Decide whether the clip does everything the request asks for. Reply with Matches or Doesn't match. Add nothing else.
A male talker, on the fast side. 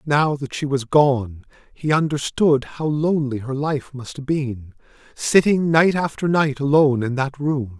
Doesn't match